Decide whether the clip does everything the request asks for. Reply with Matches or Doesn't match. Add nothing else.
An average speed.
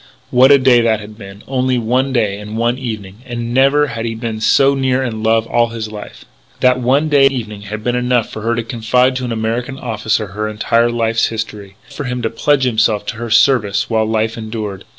Doesn't match